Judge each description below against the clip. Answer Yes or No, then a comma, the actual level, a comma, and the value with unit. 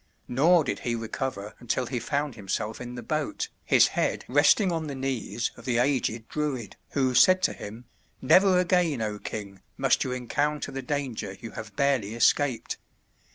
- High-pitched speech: No, low, 125 Hz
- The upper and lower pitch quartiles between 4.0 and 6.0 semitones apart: Yes, average, 4.5 semitones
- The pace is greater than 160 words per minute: Yes, average, 170 wpm